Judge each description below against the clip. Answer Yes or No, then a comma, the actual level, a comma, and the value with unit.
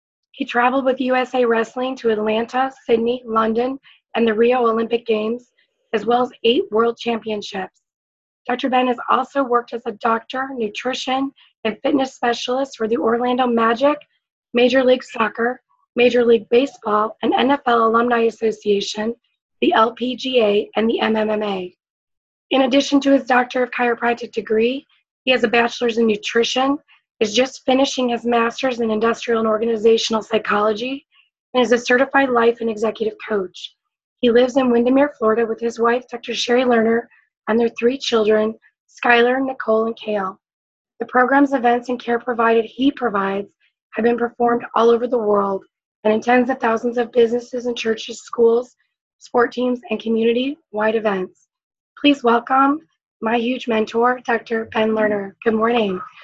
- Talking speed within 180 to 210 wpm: No, average, 155 wpm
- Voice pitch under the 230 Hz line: No, high, 235 Hz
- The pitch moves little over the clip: Yes, narrow, 2.1 semitones